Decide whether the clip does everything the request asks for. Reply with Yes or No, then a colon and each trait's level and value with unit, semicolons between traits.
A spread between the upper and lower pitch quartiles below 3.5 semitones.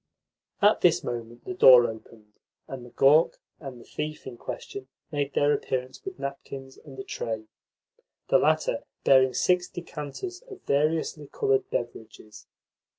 No: average, 4.2 semitones